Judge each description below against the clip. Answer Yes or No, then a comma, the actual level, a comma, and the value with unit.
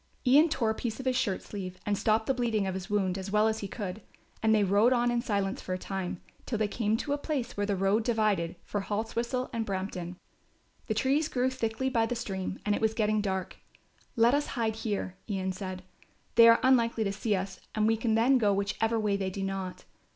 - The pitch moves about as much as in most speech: Yes, average, 3.2 semitones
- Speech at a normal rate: No, fast, 230 wpm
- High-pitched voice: Yes, high, 215 Hz